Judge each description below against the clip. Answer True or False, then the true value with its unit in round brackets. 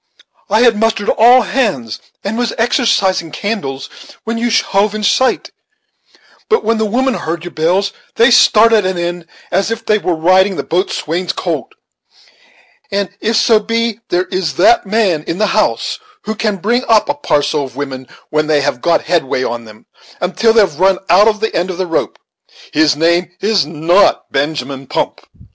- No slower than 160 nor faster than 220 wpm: True (175 wpm)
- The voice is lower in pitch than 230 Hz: True (190 Hz)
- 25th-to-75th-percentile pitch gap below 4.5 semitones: False (5.6 semitones)